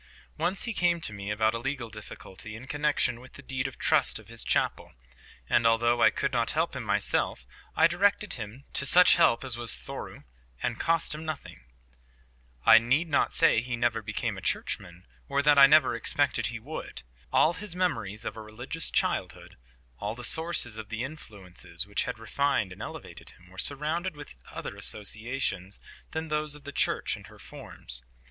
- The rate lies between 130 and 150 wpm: No, average, 185 wpm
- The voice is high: No, low, 125 Hz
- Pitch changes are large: Yes, wide, 5.9 semitones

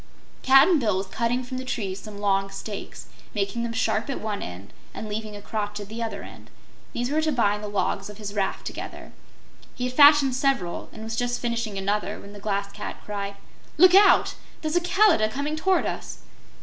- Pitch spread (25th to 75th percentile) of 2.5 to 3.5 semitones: No, average, 4.4 semitones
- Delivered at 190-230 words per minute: Yes, average, 200 wpm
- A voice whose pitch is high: Yes, high, 220 Hz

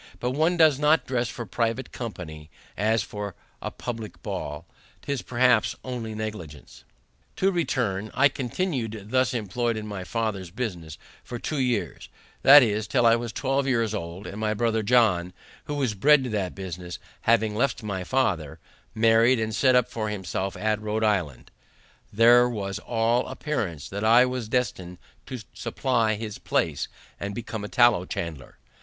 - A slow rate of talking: No, average, 160 wpm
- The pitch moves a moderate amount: Yes, average, 3.9 semitones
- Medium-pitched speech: No, low, 110 Hz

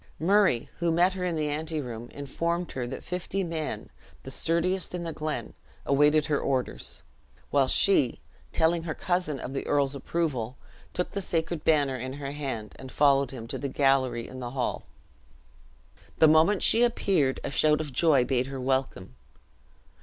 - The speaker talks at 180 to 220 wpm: No, average, 170 wpm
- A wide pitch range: No, average, 4.1 semitones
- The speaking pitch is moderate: Yes, medium, 145 Hz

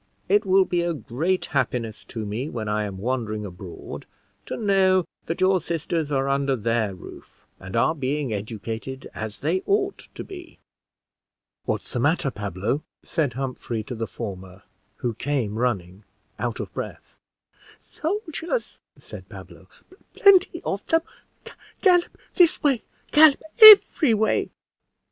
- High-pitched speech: No, low, 135 Hz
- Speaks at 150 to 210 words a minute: No, average, 140 wpm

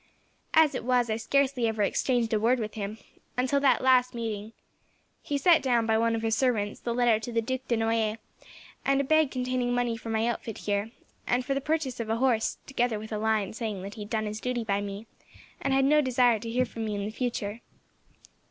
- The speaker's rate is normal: No, fast, 225 wpm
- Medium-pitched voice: No, high, 230 Hz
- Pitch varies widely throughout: No, narrow, 2.6 semitones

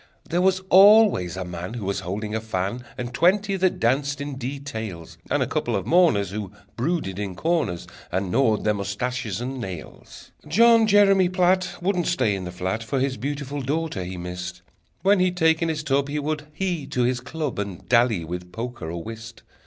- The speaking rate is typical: Yes, average, 190 wpm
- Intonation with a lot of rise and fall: Yes, wide, 8.7 semitones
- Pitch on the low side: Yes, low, 125 Hz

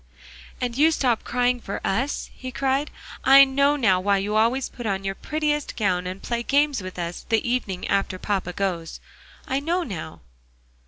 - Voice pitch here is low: No, high, 235 Hz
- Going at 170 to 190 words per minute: Yes, average, 175 wpm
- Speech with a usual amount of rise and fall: No, wide, 5.8 semitones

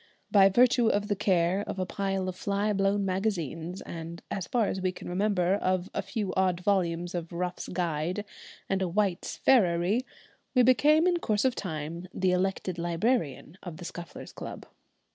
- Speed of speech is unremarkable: Yes, average, 175 wpm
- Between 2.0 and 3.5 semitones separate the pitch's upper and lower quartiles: Yes, average, 2.9 semitones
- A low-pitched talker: No, high, 190 Hz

